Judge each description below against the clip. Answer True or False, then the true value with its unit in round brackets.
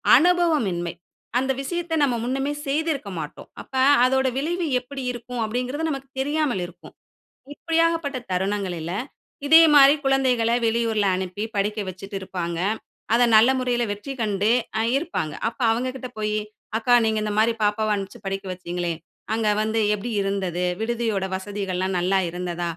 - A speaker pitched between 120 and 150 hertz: False (225 Hz)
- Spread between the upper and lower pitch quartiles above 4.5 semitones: True (5.6 semitones)